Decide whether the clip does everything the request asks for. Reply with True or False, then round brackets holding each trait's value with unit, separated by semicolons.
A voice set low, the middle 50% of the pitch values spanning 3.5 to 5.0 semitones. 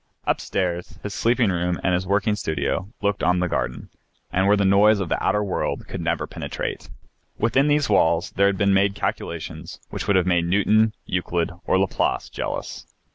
False (95 Hz; 2.5 semitones)